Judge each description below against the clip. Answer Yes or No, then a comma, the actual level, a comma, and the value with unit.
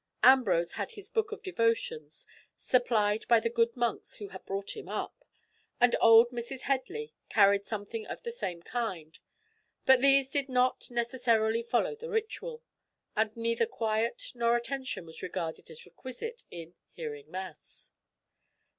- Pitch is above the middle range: Yes, high, 235 Hz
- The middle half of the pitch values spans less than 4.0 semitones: No, average, 4.5 semitones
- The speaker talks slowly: No, average, 145 wpm